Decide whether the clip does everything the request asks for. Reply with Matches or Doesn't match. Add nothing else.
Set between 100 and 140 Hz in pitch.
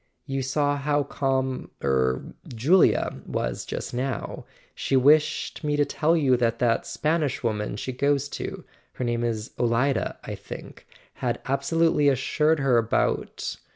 Matches